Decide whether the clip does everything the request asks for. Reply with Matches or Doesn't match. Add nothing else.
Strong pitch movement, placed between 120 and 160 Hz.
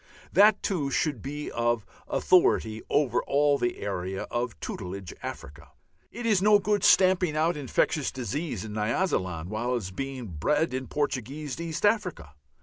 Matches